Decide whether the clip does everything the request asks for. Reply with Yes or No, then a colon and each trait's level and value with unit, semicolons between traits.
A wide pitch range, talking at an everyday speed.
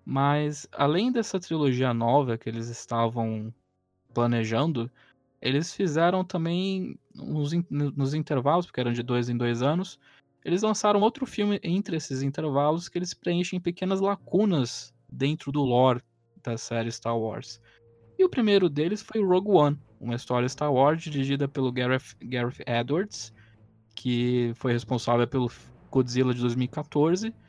Yes: wide, 6.3 semitones; average, 140 wpm